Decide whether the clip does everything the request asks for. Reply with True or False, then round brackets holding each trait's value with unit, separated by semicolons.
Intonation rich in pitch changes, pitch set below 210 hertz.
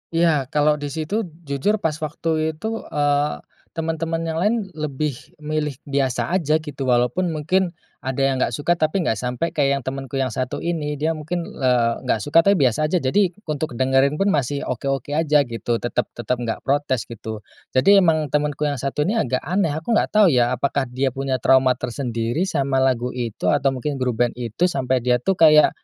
False (3.8 semitones; 140 Hz)